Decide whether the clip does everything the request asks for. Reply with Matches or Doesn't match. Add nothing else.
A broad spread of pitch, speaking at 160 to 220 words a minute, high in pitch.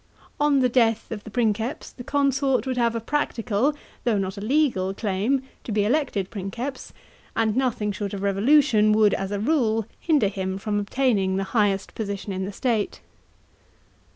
Doesn't match